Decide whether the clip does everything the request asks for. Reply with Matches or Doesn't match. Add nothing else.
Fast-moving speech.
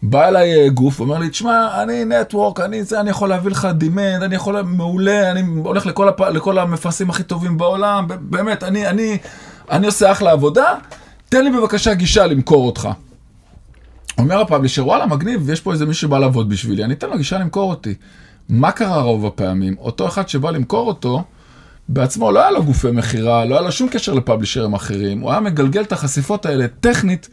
Matches